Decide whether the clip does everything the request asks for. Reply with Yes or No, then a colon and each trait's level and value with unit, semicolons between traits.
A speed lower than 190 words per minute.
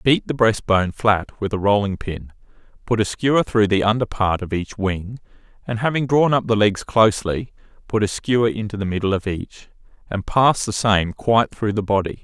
No: fast, 205 wpm